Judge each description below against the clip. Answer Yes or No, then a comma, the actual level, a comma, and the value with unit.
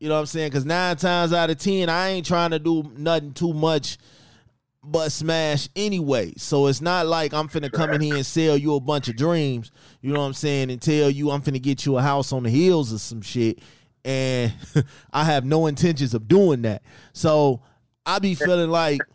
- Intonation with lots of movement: No, average, 3.4 semitones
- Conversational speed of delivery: No, fast, 225 wpm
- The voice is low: No, medium, 150 Hz